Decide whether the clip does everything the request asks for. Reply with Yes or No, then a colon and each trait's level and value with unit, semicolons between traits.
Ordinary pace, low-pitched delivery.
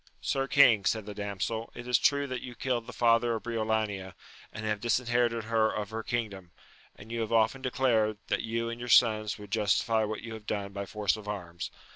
No: fast, 210 wpm; low, 110 Hz